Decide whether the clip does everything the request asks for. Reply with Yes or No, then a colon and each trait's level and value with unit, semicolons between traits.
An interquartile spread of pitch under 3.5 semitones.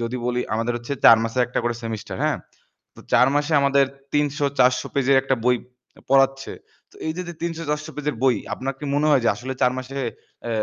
Yes: average, 2.8 semitones